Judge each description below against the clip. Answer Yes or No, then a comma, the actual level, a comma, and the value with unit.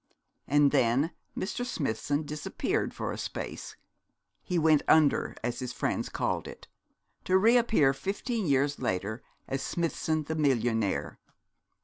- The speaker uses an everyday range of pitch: Yes, average, 4.2 semitones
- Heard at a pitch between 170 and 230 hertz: No, medium, 145 Hz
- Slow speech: Yes, slow, 130 wpm